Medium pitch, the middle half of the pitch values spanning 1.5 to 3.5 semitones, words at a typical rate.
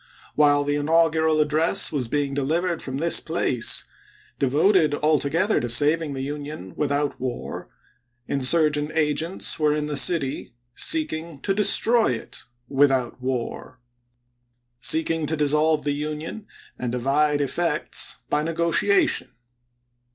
No: medium, 150 Hz; average, 2.9 semitones; slow, 120 wpm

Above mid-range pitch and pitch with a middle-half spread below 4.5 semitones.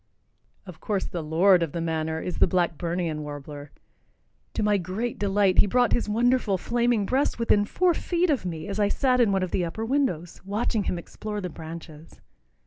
No: high, 195 Hz; average, 5.2 semitones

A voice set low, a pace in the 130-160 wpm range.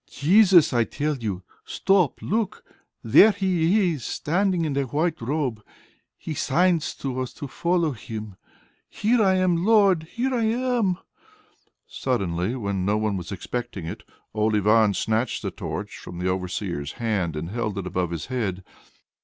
Yes: low, 130 Hz; average, 155 wpm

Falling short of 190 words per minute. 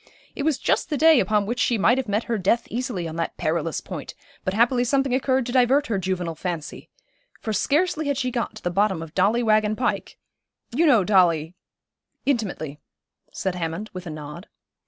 No: average, 200 wpm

